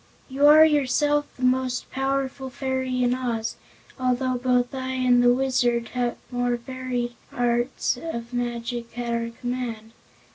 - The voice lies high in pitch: Yes, very high, 250 Hz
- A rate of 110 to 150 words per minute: Yes, average, 140 wpm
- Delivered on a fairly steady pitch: Yes, narrow, 1.4 semitones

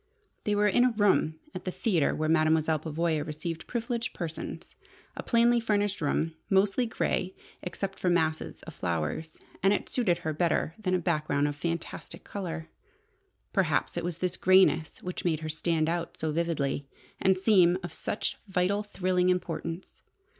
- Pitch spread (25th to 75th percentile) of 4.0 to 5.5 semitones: No, average, 3.5 semitones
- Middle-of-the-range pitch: Yes, medium, 175 Hz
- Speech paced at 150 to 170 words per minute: Yes, average, 160 wpm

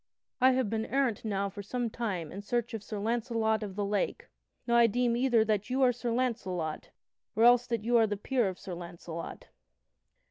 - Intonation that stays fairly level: No, average, 3.1 semitones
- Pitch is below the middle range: No, high, 225 Hz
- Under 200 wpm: No, fast, 205 wpm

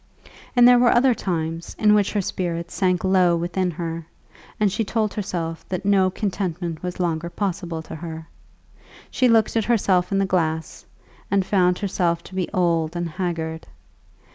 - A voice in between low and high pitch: Yes, medium, 180 Hz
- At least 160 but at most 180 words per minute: Yes, average, 170 wpm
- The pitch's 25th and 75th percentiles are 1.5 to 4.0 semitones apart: Yes, average, 3.0 semitones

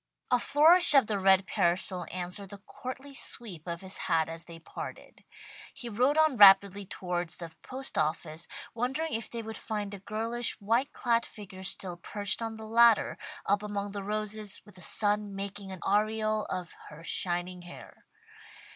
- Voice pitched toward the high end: Yes, high, 205 Hz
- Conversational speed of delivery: Yes, average, 170 wpm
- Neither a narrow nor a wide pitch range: Yes, average, 3.7 semitones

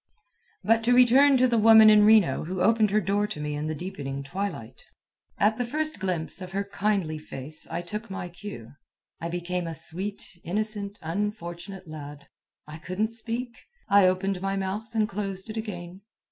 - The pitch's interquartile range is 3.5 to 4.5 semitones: Yes, average, 4.0 semitones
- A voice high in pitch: Yes, high, 195 Hz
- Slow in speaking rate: No, average, 175 wpm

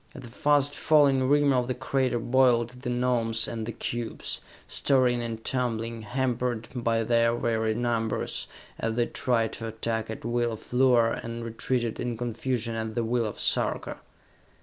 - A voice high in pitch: No, low, 120 Hz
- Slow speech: No, average, 165 wpm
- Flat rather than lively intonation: Yes, narrow, 1.8 semitones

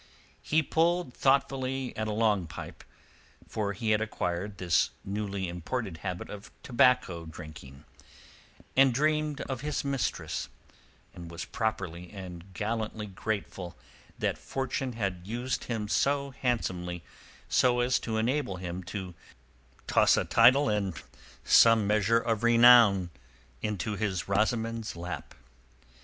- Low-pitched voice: Yes, low, 110 Hz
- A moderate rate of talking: No, slow, 120 wpm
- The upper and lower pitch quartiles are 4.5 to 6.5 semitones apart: Yes, average, 5.2 semitones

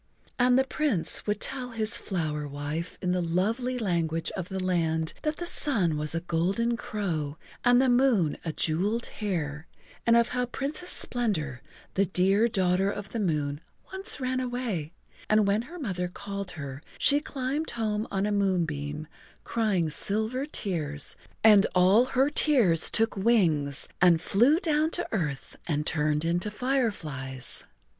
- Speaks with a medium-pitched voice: No, high, 195 Hz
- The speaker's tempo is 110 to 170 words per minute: Yes, average, 155 wpm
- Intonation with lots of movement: Yes, wide, 6.9 semitones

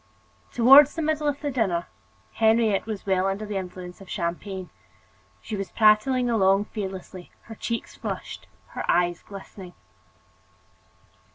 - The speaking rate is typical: No, slow, 130 wpm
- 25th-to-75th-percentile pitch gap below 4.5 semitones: Yes, average, 3.6 semitones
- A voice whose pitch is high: Yes, high, 205 Hz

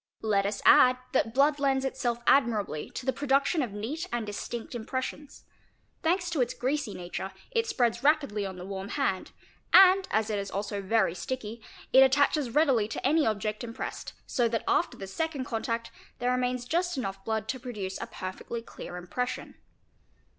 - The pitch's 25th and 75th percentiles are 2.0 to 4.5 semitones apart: No, average, 4.9 semitones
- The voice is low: No, high, 240 Hz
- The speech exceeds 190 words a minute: No, average, 175 wpm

